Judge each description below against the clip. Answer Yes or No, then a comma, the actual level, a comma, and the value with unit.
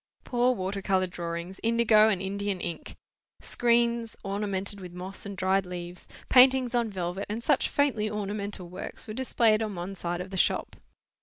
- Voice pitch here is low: No, high, 200 Hz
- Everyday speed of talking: Yes, average, 165 wpm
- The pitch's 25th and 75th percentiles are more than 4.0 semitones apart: No, average, 3.4 semitones